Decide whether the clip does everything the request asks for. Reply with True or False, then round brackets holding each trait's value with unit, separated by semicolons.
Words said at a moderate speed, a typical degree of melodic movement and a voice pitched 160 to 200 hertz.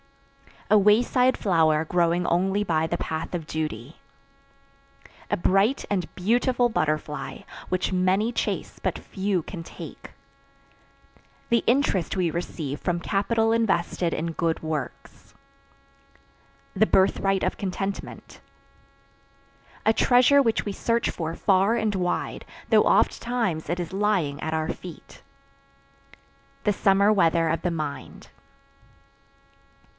False (120 wpm; 4.2 semitones; 185 Hz)